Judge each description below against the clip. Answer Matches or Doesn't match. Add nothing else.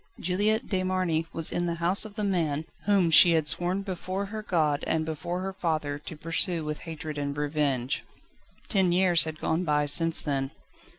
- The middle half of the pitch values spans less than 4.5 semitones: Matches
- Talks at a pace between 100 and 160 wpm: Doesn't match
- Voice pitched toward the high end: Doesn't match